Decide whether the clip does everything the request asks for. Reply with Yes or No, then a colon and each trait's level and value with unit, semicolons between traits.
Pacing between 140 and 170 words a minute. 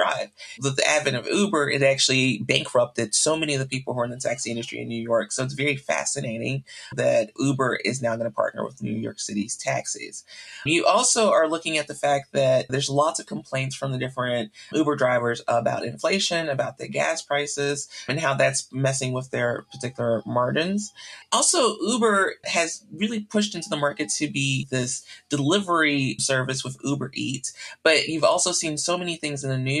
No: average, 195 wpm